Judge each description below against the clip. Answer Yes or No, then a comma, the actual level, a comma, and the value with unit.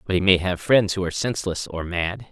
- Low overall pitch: Yes, very low, 95 Hz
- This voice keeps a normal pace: No, fast, 260 wpm